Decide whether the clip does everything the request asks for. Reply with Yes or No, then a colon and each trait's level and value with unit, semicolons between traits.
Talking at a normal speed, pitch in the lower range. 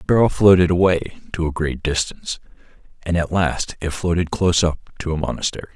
Yes: average, 190 wpm; very low, 85 Hz